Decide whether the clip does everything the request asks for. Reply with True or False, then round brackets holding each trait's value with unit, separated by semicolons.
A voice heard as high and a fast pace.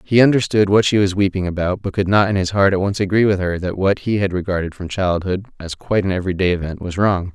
False (95 Hz; 260 wpm)